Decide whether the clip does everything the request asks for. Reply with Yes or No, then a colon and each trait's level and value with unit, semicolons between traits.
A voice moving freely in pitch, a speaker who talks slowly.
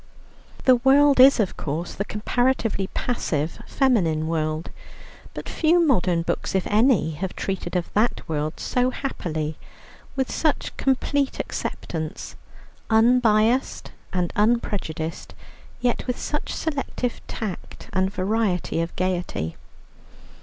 Yes: wide, 7.0 semitones; slow, 115 wpm